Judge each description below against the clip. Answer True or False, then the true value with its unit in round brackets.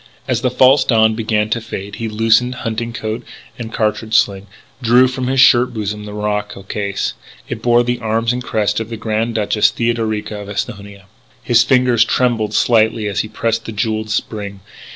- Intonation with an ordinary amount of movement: False (2.0 semitones)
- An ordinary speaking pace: True (180 wpm)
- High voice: False (110 Hz)